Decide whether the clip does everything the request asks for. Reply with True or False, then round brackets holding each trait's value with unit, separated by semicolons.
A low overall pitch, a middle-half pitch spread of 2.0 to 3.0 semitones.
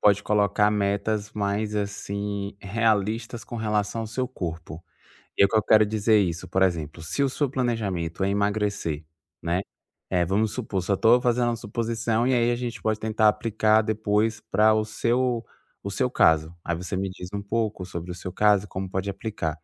True (105 Hz; 2.7 semitones)